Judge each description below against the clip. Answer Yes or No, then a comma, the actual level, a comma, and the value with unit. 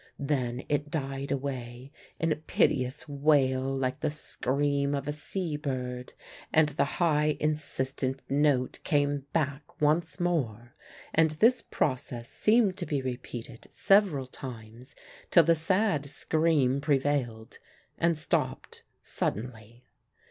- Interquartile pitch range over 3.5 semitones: No, average, 3.1 semitones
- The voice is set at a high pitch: No, medium, 140 Hz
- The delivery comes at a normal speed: No, slow, 120 wpm